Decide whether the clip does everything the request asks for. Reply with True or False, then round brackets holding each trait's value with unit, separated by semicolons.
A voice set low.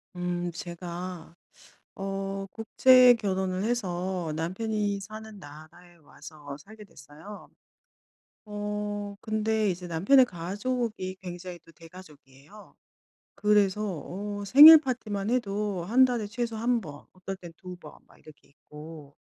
False (195 Hz)